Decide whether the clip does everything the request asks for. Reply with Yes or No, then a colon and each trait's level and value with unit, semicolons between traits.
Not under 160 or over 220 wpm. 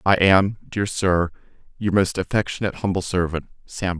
No: average, 150 wpm